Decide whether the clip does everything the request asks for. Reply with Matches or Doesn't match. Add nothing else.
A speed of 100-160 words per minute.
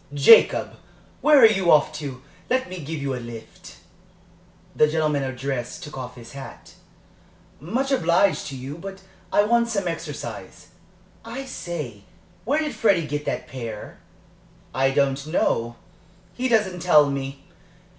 Matches